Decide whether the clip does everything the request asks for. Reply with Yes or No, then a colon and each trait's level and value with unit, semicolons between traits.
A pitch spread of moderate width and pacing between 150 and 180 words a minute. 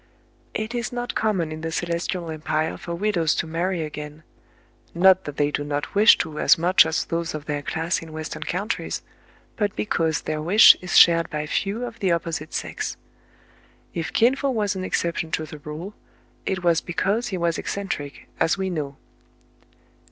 No: average, 3.7 semitones; average, 190 wpm